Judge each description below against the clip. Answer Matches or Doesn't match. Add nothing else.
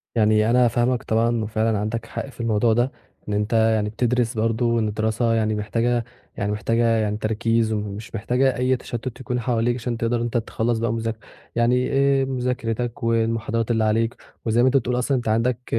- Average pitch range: Doesn't match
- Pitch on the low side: Matches